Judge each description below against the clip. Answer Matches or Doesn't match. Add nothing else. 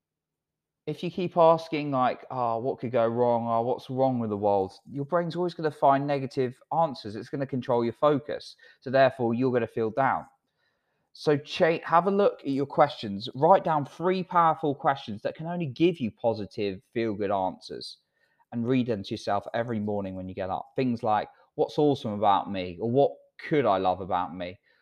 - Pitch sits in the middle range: Doesn't match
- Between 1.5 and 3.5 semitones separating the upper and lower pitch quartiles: Doesn't match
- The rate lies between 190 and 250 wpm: Matches